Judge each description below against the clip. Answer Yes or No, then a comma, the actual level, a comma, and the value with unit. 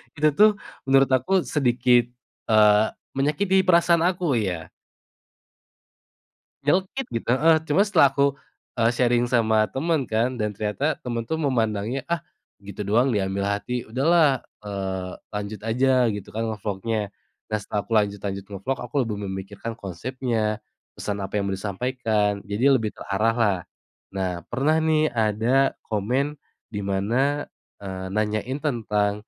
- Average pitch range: Yes, average, 4.8 semitones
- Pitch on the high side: No, low, 115 Hz